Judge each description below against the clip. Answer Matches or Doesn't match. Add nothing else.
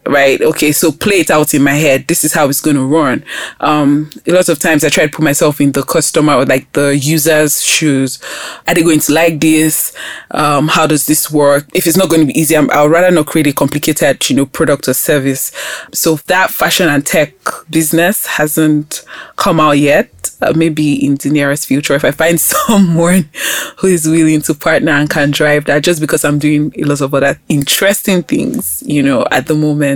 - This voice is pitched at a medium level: Matches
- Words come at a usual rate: Doesn't match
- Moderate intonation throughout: Doesn't match